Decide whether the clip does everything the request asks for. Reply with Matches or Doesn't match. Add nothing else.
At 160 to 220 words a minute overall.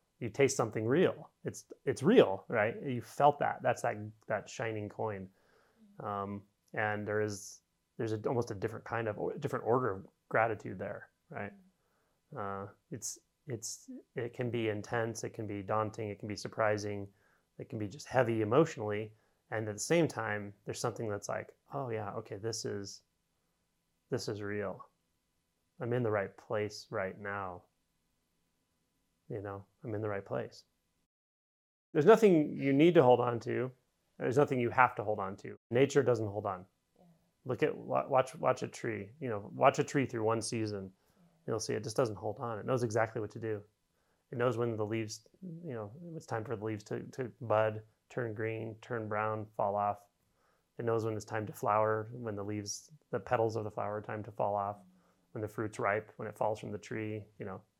Matches